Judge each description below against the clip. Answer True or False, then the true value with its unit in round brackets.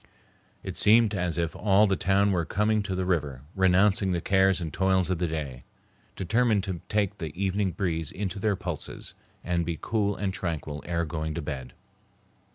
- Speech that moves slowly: False (180 wpm)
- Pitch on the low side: True (95 Hz)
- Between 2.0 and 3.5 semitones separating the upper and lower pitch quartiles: True (3.2 semitones)